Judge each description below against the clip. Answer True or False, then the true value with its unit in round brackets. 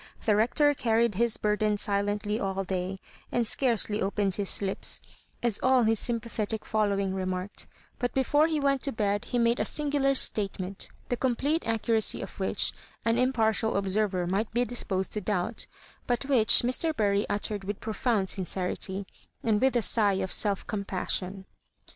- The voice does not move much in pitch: False (3.3 semitones)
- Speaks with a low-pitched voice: False (215 Hz)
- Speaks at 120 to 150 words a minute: False (160 wpm)